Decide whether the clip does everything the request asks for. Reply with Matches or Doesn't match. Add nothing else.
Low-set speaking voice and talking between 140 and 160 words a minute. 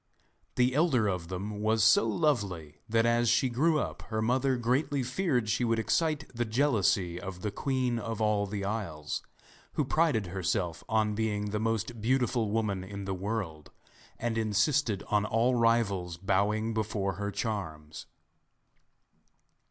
Matches